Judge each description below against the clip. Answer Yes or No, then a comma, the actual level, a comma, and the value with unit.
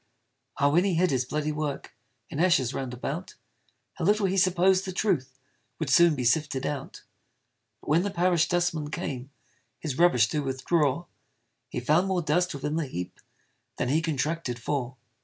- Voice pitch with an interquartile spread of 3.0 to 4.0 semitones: No, average, 4.7 semitones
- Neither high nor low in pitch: Yes, medium, 155 Hz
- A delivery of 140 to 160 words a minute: No, average, 170 wpm